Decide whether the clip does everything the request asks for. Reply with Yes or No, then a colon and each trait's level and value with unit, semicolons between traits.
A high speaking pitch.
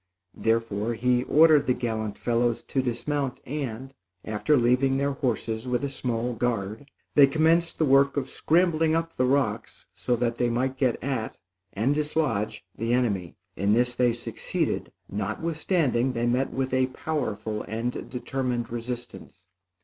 No: low, 125 Hz